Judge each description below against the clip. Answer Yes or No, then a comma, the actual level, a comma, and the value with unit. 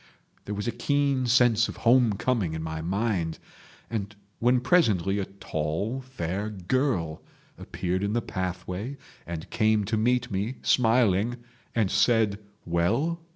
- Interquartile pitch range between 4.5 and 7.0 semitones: Yes, average, 4.9 semitones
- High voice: No, low, 105 Hz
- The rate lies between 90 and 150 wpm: Yes, average, 140 wpm